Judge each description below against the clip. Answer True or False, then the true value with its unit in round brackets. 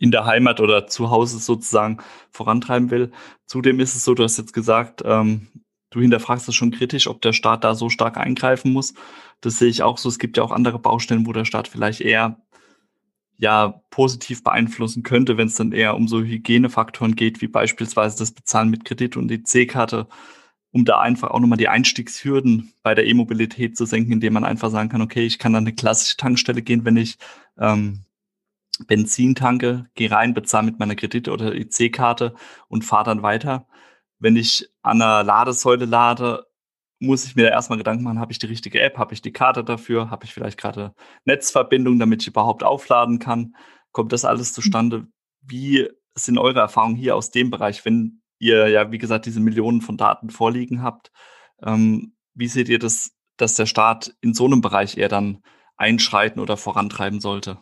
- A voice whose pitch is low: True (115 Hz)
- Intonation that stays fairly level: True (1.7 semitones)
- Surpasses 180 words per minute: True (190 wpm)